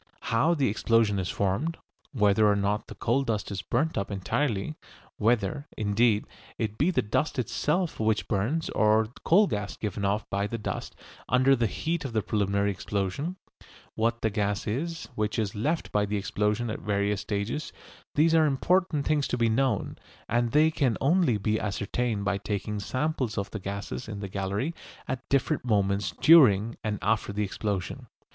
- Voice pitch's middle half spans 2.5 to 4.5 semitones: No, average, 5.0 semitones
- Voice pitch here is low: Yes, low, 110 Hz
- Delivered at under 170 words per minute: No, average, 175 wpm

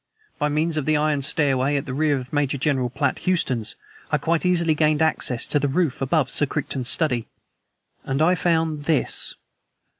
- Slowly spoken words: No, average, 180 wpm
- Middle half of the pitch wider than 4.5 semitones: No, average, 2.9 semitones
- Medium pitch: Yes, medium, 150 Hz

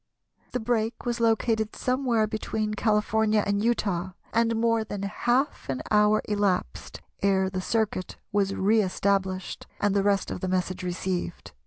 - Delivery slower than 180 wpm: Yes, average, 150 wpm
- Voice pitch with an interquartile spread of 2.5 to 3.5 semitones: Yes, average, 2.8 semitones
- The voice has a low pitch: No, high, 210 Hz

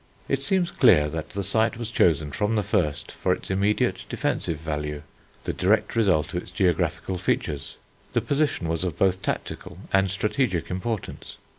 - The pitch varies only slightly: No, average, 4.8 semitones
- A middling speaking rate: Yes, average, 165 wpm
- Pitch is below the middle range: Yes, very low, 95 Hz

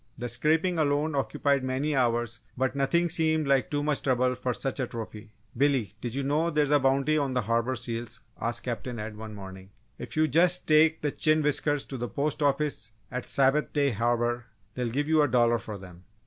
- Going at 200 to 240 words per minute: Yes, fast, 205 wpm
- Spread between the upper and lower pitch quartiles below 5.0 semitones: Yes, average, 3.9 semitones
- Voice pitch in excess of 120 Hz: Yes, low, 135 Hz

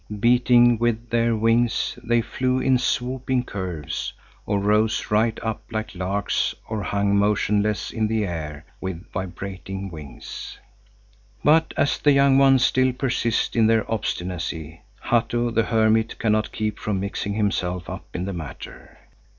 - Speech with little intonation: No, average, 3.5 semitones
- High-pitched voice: No, low, 110 Hz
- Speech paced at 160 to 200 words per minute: No, average, 140 wpm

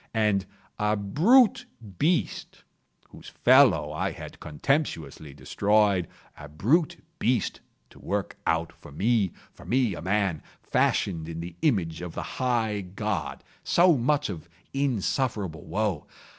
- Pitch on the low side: Yes, low, 105 Hz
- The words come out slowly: Yes, slow, 115 wpm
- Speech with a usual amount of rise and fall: No, wide, 7.1 semitones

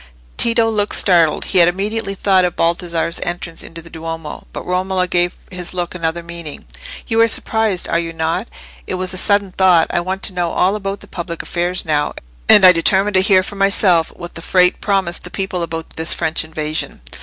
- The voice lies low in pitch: No, medium, 180 Hz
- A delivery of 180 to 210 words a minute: Yes, average, 200 wpm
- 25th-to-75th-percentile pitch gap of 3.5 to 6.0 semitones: No, narrow, 2.5 semitones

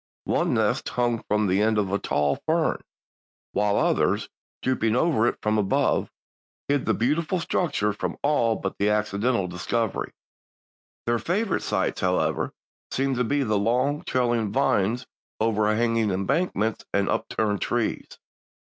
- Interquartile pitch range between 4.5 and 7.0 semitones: No, average, 3.8 semitones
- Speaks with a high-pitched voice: No, low, 115 Hz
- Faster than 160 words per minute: No, slow, 135 wpm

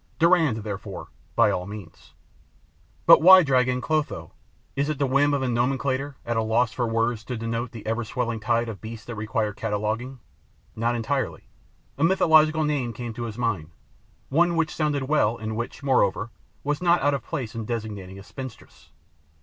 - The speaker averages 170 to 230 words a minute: Yes, average, 180 wpm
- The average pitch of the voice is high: No, low, 120 Hz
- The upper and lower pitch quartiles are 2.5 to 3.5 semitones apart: No, average, 4.3 semitones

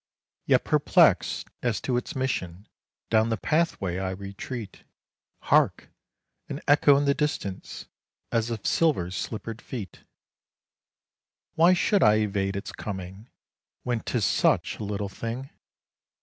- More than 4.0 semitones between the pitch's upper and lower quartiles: Yes, average, 5.1 semitones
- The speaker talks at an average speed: No, slow, 125 wpm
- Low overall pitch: Yes, low, 110 Hz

